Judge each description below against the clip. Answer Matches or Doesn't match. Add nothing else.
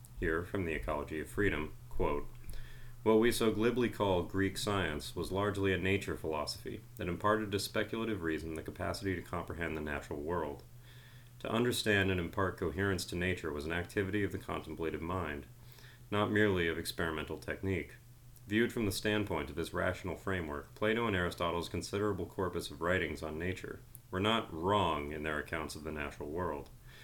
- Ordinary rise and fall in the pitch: Matches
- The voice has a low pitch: Matches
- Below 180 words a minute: Matches